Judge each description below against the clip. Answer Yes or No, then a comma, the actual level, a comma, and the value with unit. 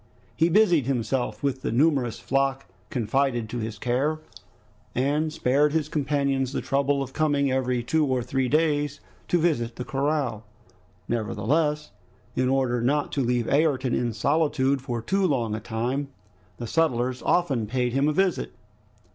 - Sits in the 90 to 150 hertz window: Yes, low, 135 Hz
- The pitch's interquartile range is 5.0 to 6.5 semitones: No, average, 3.5 semitones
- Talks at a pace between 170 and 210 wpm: No, average, 155 wpm